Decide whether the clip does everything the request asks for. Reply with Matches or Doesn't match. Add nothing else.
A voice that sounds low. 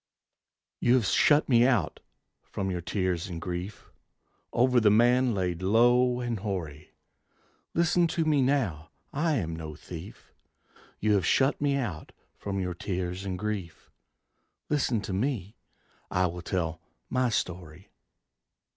Matches